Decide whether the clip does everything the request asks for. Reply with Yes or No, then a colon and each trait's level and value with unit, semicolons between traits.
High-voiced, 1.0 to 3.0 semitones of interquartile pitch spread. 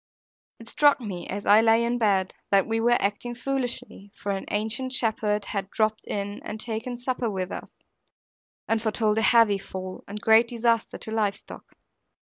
Yes: high, 220 Hz; narrow, 2.5 semitones